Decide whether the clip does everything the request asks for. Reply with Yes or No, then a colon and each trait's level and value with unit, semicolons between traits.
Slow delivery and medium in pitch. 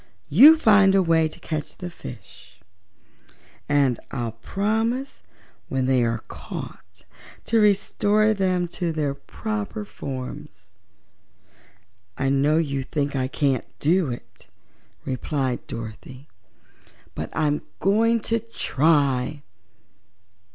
Yes: slow, 110 wpm; medium, 155 Hz